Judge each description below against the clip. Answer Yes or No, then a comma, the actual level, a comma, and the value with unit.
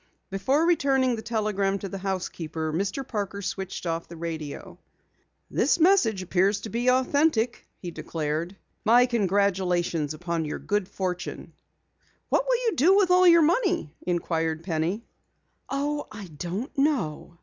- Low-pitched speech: No, high, 200 Hz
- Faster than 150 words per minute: No, average, 140 wpm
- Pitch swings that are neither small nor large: No, wide, 7.3 semitones